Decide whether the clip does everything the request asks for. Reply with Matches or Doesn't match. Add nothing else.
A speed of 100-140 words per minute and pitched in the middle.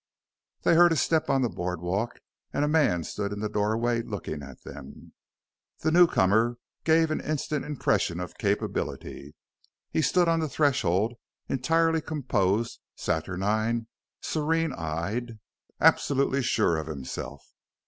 Doesn't match